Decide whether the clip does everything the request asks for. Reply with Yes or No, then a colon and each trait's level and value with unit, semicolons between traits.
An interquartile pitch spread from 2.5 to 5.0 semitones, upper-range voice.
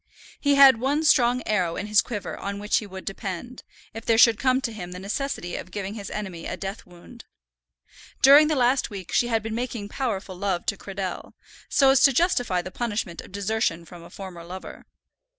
Yes: average, 4.7 semitones; high, 210 Hz